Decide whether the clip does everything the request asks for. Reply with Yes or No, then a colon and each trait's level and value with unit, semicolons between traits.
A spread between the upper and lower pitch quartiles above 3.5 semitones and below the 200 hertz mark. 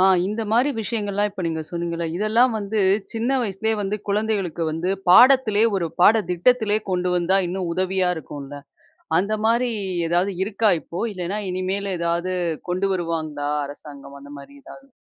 Yes: average, 4.0 semitones; high, 190 Hz